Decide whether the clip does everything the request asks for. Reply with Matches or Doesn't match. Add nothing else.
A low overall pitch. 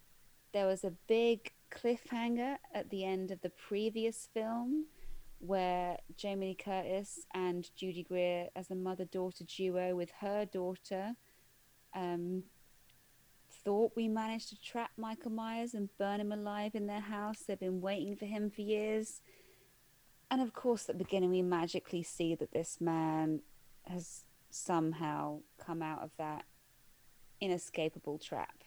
Doesn't match